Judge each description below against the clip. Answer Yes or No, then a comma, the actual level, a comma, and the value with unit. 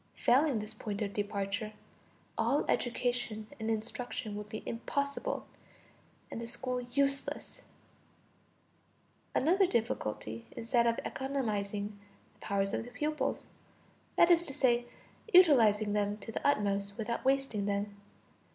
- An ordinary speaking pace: No, slow, 125 wpm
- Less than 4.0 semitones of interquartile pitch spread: No, average, 4.3 semitones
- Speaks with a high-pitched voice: Yes, high, 230 Hz